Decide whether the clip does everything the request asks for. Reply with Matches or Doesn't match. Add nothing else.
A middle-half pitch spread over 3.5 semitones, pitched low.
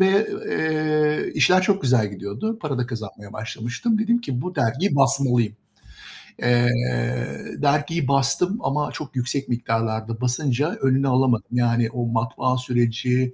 Matches